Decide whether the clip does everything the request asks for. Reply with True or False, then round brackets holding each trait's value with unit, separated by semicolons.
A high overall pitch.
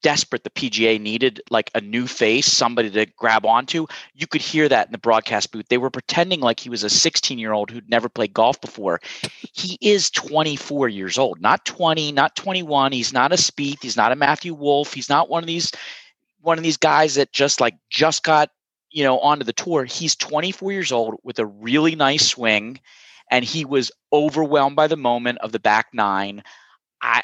False (140 Hz)